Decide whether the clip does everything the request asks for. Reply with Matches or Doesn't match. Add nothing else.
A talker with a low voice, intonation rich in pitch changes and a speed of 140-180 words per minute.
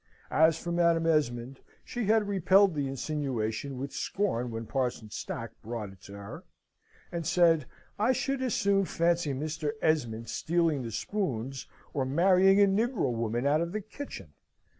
Doesn't match